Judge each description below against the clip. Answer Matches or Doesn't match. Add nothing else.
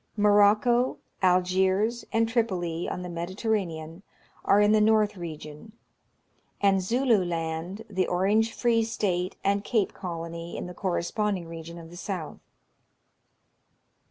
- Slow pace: Matches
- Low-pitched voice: Doesn't match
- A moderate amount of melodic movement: Matches